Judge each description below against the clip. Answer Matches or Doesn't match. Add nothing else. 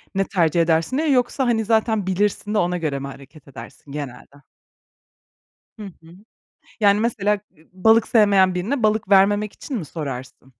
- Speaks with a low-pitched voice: Doesn't match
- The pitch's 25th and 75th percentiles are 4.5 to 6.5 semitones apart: Matches